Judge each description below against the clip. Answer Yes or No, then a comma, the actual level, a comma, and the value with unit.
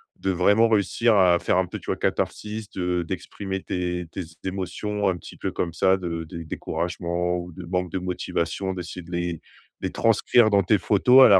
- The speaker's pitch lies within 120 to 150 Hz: No, very low, 90 Hz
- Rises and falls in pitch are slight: Yes, narrow, 2.2 semitones